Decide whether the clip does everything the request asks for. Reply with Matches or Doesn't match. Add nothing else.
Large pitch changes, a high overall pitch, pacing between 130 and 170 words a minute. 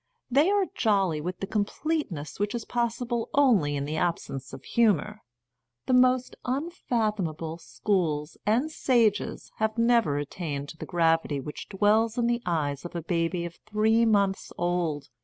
Matches